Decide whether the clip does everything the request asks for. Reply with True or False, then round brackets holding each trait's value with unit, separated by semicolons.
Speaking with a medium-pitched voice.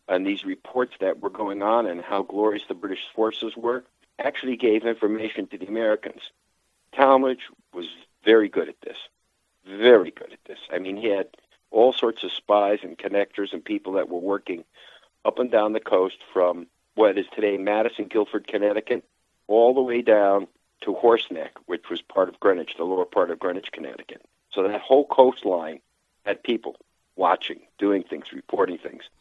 False (110 Hz)